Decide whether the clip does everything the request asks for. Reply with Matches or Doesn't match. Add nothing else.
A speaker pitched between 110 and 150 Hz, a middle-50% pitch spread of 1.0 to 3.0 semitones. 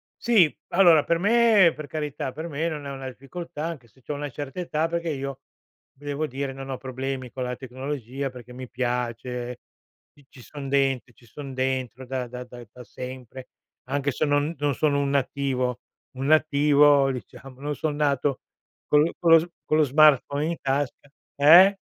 Matches